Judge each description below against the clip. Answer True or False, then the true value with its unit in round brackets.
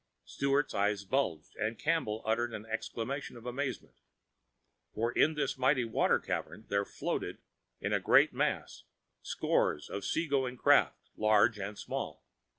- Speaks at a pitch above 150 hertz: False (115 Hz)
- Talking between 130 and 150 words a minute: True (145 wpm)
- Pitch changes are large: False (4.4 semitones)